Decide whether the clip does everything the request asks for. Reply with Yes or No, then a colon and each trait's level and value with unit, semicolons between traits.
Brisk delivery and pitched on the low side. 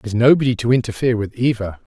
Yes: fast, 210 wpm; low, 115 Hz